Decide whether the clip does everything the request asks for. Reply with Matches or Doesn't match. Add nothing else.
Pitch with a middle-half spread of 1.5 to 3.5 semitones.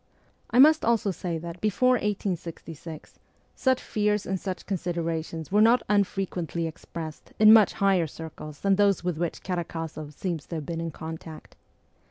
Doesn't match